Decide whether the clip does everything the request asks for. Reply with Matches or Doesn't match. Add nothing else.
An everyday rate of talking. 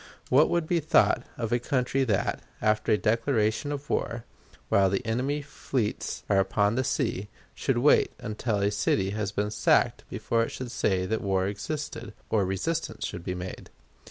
Matches